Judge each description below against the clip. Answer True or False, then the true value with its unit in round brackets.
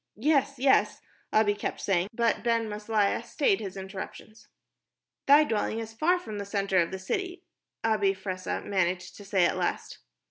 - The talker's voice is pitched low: False (210 Hz)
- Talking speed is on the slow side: False (165 wpm)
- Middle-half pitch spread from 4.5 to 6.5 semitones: False (3.3 semitones)